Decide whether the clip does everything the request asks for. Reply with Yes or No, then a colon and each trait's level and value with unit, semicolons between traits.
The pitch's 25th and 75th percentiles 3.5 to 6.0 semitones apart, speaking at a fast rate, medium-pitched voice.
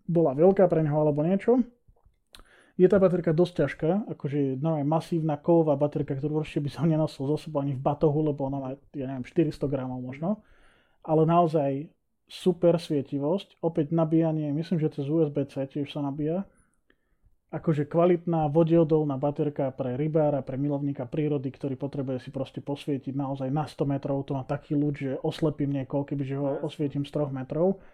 No: narrow, 2.5 semitones; fast, 170 wpm; medium, 150 Hz